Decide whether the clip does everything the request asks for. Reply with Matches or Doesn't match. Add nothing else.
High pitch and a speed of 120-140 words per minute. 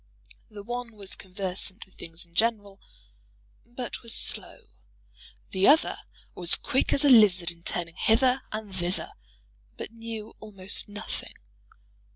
Matches